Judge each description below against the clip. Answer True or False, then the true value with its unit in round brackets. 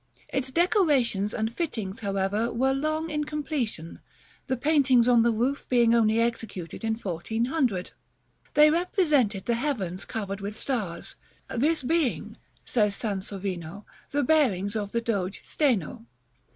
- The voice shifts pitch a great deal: True (5.9 semitones)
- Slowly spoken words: True (130 wpm)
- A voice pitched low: False (235 Hz)